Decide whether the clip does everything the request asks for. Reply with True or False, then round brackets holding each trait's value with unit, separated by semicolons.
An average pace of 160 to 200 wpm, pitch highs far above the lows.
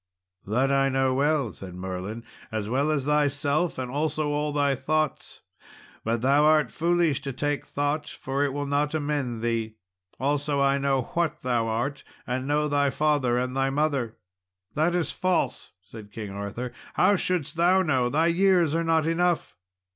False (170 wpm; 3.5 semitones)